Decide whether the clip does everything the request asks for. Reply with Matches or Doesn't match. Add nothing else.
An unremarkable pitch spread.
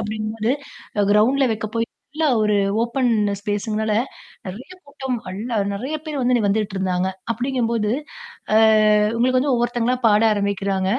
Matches